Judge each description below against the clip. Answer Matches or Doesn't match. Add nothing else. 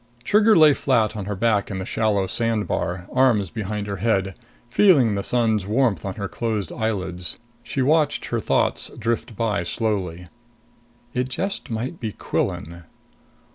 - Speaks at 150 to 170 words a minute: Matches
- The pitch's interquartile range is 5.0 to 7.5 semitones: Doesn't match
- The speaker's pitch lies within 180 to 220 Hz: Doesn't match